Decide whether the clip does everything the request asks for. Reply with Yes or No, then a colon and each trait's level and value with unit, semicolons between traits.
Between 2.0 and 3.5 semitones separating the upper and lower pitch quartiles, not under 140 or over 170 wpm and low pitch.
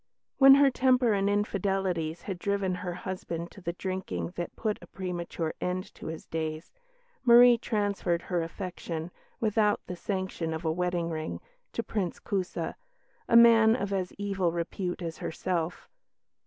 No: average, 3.2 semitones; average, 155 wpm; medium, 185 Hz